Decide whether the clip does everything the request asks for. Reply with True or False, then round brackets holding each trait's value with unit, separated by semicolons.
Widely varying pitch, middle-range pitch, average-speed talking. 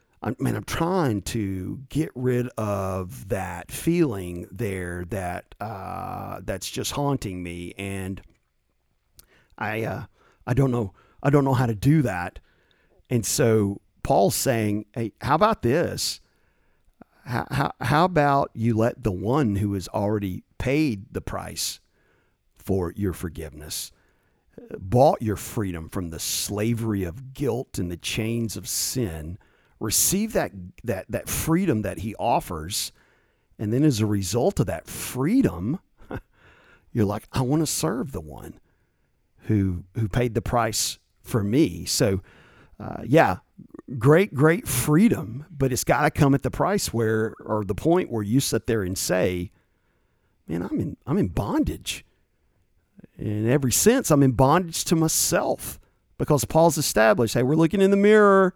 False (6.1 semitones; 115 Hz; 150 wpm)